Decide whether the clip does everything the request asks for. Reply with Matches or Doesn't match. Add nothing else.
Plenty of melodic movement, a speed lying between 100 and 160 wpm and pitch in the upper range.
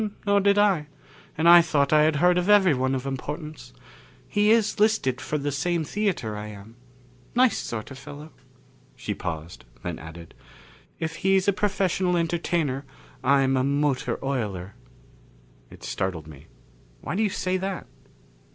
Doesn't match